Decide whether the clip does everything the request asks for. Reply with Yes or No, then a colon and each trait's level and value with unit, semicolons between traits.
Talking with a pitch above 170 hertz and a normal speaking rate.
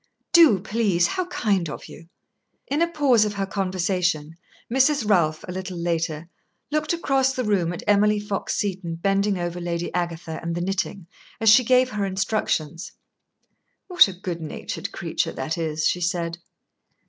Yes: high, 190 Hz; average, 160 wpm